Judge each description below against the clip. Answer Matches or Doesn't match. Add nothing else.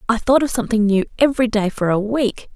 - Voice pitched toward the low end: Doesn't match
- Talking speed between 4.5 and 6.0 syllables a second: Doesn't match